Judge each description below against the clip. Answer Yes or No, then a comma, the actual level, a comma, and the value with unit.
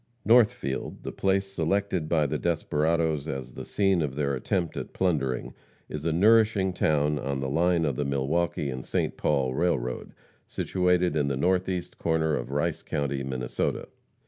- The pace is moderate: Yes, average, 160 wpm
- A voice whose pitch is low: Yes, very low, 80 Hz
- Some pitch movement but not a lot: Yes, average, 4.5 semitones